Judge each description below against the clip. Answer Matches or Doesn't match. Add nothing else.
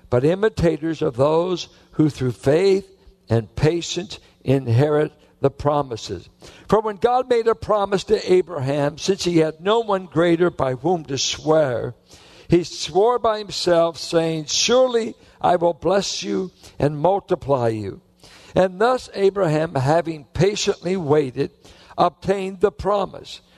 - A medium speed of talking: Doesn't match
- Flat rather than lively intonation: Doesn't match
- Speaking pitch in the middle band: Matches